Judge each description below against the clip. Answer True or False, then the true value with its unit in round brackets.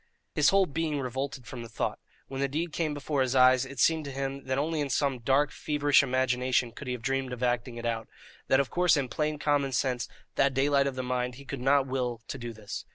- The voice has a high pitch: False (135 Hz)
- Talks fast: True (240 wpm)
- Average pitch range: False (2.3 semitones)